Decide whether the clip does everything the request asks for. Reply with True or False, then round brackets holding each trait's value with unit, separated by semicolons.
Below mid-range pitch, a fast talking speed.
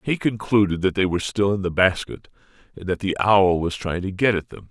True (100 Hz; 240 wpm)